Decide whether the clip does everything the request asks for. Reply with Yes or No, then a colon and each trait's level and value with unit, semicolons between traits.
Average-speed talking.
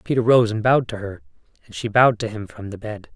No: fast, 265 wpm